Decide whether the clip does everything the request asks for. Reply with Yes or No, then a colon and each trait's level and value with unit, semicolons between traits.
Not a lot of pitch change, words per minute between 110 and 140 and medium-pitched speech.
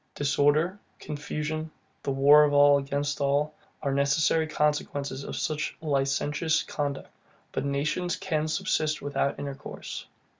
Yes: narrow, 1.5 semitones; slow, 135 wpm; medium, 145 Hz